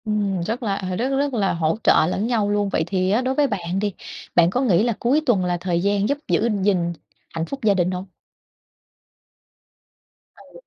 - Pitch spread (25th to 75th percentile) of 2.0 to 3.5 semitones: No, average, 4.4 semitones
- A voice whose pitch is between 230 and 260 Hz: No, high, 200 Hz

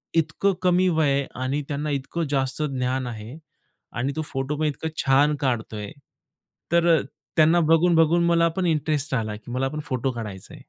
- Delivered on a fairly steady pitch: No, average, 3.8 semitones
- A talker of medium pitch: Yes, medium, 145 Hz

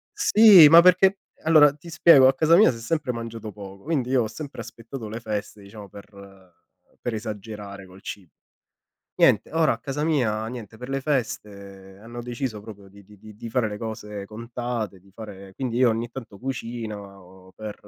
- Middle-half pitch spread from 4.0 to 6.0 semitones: Yes, average, 4.5 semitones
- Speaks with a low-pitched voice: Yes, low, 115 Hz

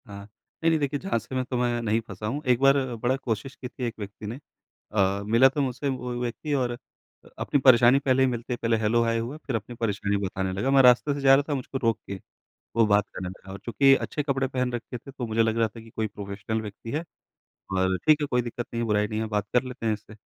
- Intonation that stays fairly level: No, average, 3.7 semitones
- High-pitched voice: No, low, 120 Hz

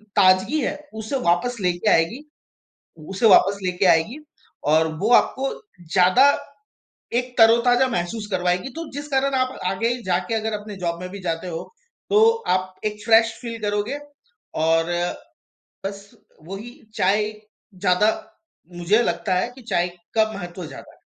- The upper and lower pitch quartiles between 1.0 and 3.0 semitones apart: No, average, 4.5 semitones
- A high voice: Yes, high, 205 Hz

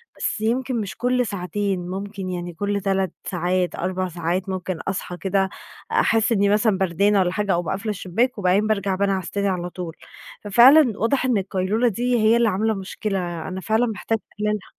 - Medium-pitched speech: No, high, 200 Hz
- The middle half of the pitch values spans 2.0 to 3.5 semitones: Yes, average, 2.9 semitones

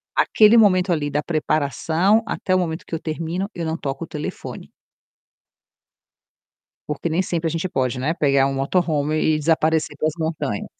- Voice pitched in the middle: Yes, medium, 160 Hz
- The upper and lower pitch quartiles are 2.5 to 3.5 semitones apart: Yes, average, 2.9 semitones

